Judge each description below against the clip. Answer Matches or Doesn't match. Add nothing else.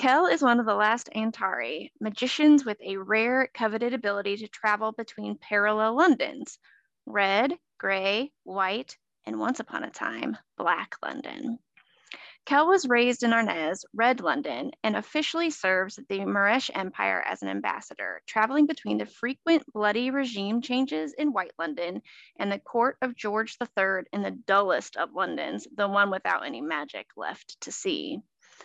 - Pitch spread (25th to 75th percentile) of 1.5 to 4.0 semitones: Doesn't match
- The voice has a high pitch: Matches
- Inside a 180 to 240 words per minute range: Doesn't match